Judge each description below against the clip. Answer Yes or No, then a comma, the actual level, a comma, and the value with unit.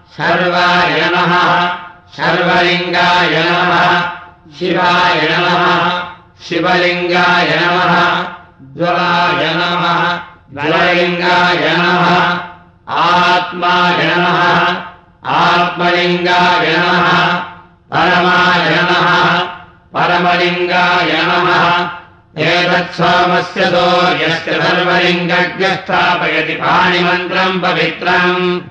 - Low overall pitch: No, medium, 175 Hz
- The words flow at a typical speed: No, slow, 50 wpm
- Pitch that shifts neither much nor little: No, narrow, 0.3 semitones